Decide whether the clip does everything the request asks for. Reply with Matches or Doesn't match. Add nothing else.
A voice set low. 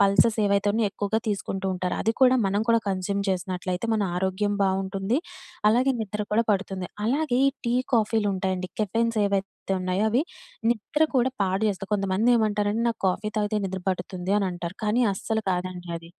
Doesn't match